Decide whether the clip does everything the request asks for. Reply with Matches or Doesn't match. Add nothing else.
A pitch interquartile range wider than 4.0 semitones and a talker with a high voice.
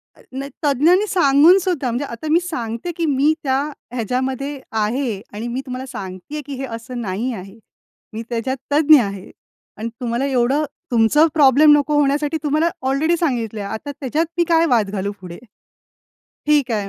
Matches